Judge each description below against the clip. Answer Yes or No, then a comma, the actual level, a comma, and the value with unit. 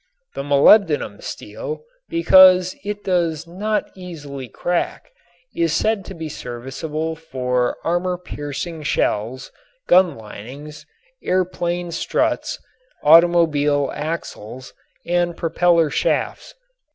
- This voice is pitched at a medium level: Yes, medium, 165 Hz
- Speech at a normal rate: No, slow, 100 wpm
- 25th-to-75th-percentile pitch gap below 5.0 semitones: Yes, average, 3.8 semitones